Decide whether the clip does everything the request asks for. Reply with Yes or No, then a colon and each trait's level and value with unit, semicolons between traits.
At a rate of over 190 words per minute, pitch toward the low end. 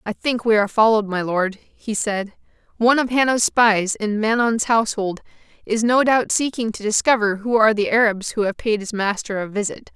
No: average, 200 wpm; high, 220 Hz